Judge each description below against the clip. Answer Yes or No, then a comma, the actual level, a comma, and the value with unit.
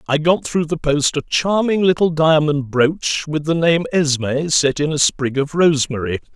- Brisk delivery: No, average, 190 wpm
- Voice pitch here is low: No, medium, 155 Hz